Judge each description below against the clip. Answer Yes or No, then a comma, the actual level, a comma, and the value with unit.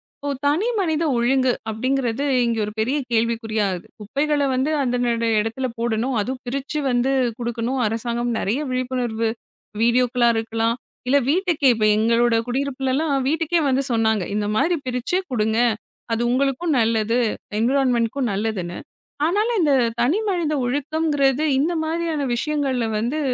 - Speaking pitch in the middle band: No, very high, 255 Hz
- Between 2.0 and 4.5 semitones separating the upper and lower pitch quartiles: Yes, average, 3.9 semitones